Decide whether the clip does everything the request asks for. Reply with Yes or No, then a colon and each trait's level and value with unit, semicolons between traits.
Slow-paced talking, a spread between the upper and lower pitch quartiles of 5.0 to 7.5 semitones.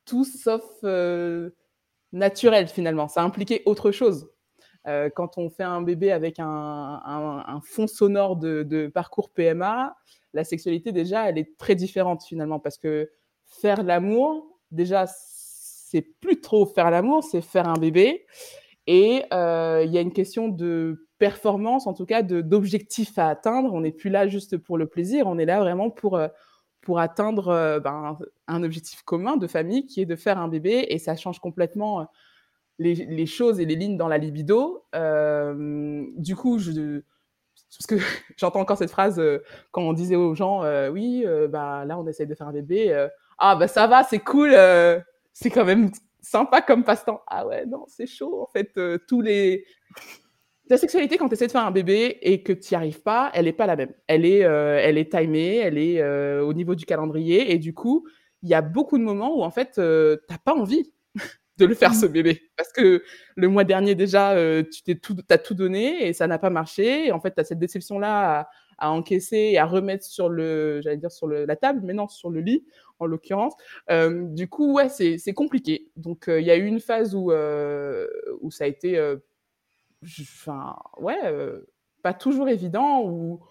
No: average, 200 wpm; wide, 5.5 semitones